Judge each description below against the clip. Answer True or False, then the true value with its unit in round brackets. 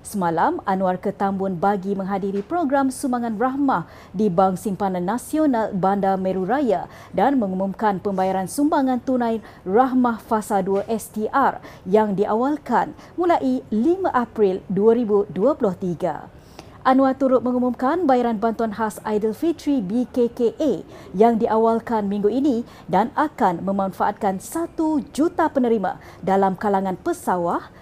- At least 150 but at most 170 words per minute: False (110 wpm)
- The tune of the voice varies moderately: True (4.8 semitones)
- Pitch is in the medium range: False (220 Hz)